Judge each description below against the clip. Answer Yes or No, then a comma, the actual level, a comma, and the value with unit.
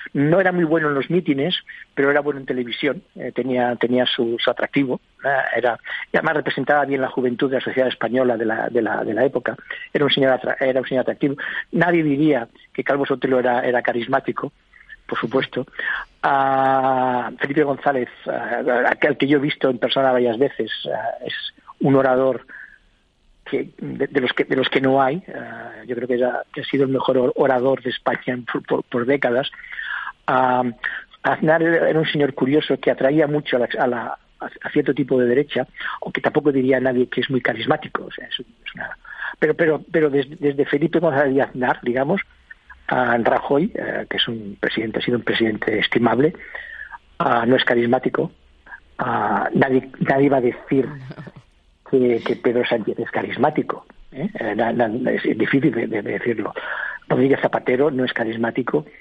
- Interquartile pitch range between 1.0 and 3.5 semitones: Yes, average, 2.7 semitones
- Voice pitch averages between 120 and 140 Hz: Yes, low, 135 Hz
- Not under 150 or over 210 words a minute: Yes, average, 180 wpm